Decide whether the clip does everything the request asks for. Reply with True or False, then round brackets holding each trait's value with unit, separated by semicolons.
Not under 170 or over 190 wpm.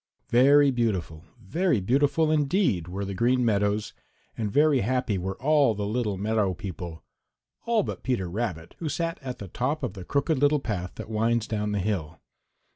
True (175 wpm)